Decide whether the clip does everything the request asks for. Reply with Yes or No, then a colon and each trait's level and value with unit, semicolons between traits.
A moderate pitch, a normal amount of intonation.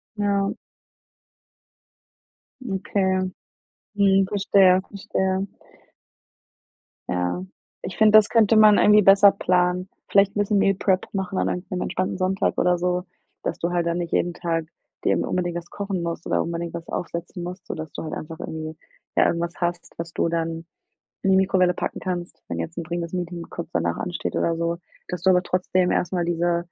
No: medium, 180 Hz; narrow, 2.2 semitones